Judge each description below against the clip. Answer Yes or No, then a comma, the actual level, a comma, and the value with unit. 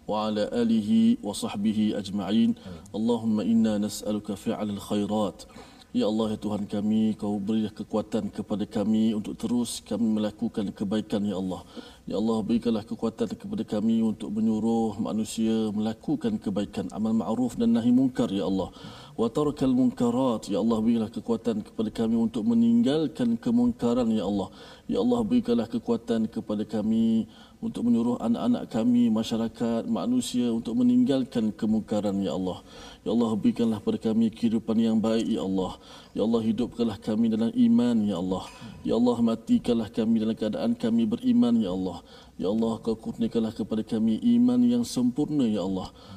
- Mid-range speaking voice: No, high, 230 Hz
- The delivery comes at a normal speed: No, fast, 150 wpm